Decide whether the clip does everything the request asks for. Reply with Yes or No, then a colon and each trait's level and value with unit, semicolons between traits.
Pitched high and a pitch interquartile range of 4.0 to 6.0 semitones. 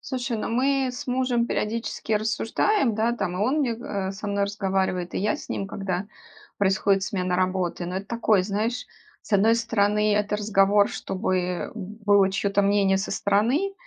No: high, 205 Hz; average, 2.9 semitones